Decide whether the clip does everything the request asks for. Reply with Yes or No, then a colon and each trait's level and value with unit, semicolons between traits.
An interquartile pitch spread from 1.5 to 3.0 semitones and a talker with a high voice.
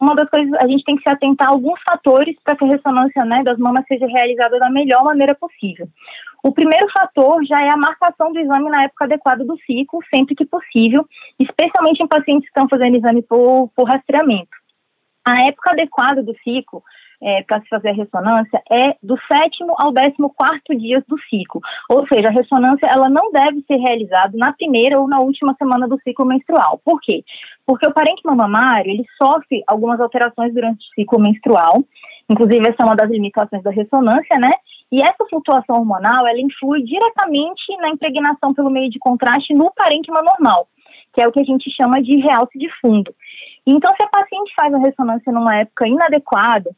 No: average, 3.8 semitones; very high, 270 Hz